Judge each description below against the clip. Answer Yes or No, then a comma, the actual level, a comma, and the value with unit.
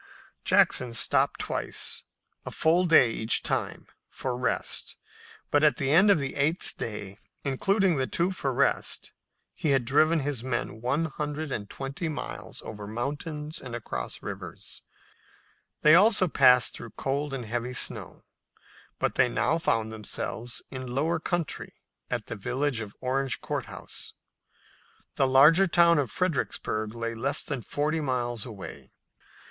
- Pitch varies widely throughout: No, average, 4.6 semitones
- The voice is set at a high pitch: No, low, 135 Hz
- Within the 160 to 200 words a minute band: No, average, 145 wpm